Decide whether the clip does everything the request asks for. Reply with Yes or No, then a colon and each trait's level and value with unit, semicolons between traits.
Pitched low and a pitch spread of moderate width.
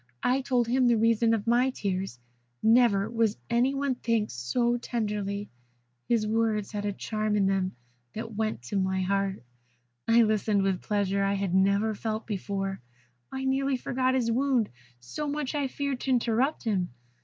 No: high, 220 Hz; average, 3.7 semitones